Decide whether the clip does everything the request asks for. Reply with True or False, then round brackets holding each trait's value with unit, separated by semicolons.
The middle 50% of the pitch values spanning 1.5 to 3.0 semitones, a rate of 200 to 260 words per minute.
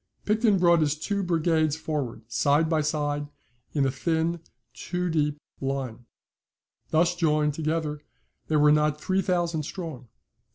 False (2.5 semitones; 135 wpm)